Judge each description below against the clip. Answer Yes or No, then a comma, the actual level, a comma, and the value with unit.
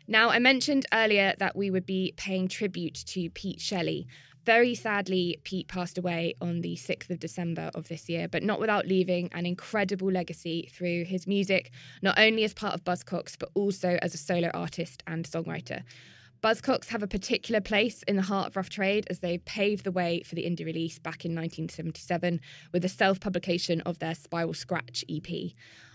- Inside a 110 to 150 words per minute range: No, average, 190 wpm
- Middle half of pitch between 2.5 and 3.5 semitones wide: Yes, average, 2.9 semitones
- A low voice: No, medium, 180 Hz